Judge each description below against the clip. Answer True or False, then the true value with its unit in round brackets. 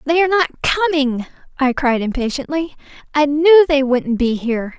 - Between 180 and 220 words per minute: False (165 wpm)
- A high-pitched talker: True (285 Hz)